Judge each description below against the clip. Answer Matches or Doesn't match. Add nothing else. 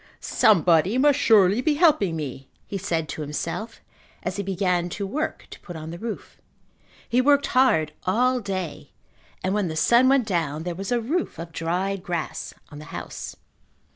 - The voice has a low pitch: Doesn't match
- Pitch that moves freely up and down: Matches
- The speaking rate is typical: Matches